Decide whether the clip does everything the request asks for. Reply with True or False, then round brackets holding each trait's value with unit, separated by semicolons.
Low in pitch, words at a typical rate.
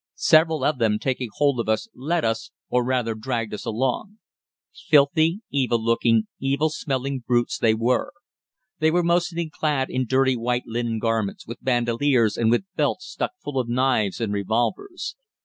True (125 Hz; 165 wpm)